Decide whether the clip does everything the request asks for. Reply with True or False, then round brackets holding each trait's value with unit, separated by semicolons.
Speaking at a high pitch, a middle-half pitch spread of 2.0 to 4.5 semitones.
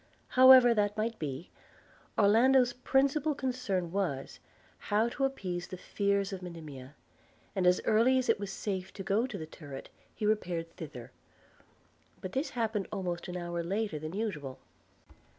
False (200 Hz; 5.1 semitones)